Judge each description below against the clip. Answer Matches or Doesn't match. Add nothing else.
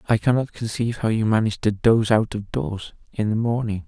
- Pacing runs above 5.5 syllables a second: Matches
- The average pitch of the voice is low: Matches